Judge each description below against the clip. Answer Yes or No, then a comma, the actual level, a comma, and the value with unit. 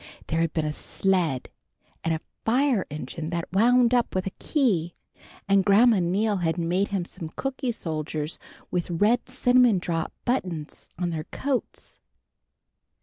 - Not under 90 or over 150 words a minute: Yes, average, 145 wpm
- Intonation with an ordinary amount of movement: No, wide, 6.1 semitones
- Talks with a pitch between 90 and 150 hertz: No, medium, 185 Hz